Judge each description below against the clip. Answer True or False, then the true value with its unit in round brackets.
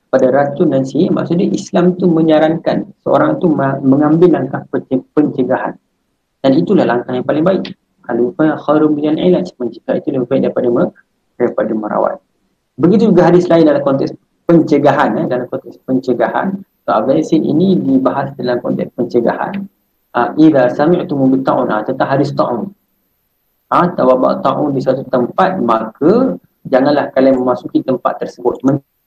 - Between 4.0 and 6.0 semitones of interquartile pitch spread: True (4.5 semitones)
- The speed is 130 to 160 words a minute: True (150 wpm)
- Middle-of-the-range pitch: True (145 Hz)